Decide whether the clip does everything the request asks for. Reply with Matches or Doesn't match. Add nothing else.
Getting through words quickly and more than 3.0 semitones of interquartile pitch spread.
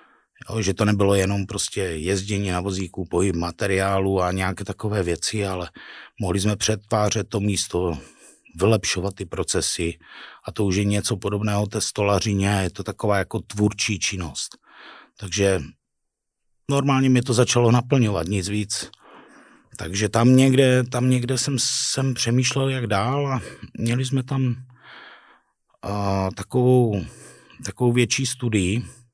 Doesn't match